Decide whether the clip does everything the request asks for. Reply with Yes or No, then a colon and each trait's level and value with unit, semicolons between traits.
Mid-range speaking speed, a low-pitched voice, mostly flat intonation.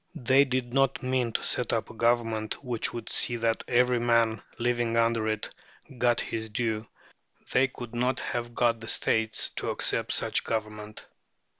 Yes: average, 170 wpm; low, 115 Hz; narrow, 1.6 semitones